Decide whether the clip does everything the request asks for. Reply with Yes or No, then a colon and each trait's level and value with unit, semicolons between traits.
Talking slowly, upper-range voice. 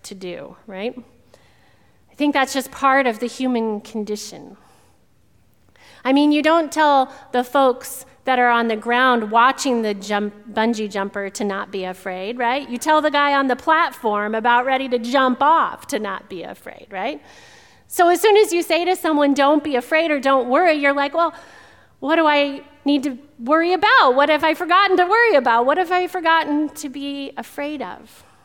No: average, 190 wpm; very high, 270 Hz